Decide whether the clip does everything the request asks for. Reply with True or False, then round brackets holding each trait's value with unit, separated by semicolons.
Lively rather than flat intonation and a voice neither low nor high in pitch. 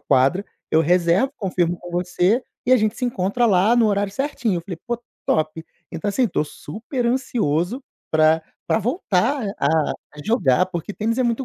False (5.7 semitones; 200 Hz)